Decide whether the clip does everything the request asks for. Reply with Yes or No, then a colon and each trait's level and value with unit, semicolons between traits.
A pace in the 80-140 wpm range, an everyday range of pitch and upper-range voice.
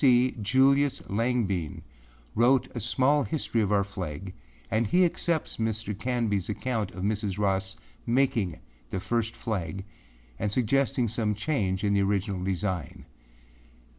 No: slow, 135 wpm; average, 4.2 semitones; low, 105 Hz